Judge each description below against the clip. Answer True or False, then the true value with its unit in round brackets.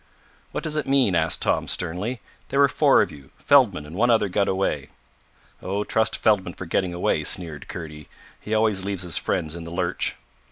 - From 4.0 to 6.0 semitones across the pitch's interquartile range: True (4.6 semitones)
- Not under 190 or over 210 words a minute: True (195 wpm)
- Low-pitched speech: True (95 Hz)